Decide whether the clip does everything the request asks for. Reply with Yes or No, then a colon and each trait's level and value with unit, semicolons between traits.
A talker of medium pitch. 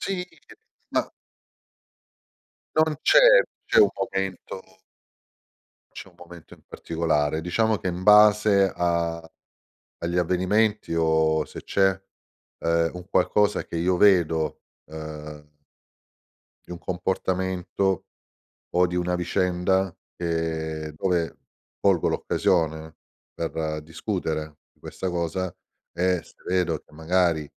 No: very low, 90 Hz